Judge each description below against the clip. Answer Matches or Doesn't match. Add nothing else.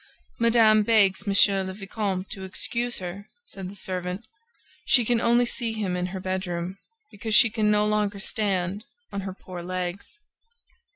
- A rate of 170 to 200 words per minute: Doesn't match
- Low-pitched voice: Doesn't match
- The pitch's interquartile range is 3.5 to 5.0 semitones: Doesn't match